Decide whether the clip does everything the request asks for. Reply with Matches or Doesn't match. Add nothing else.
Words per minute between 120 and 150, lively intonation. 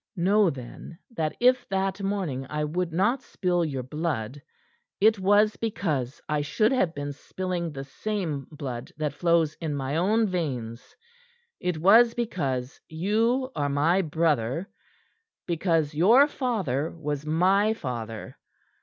Matches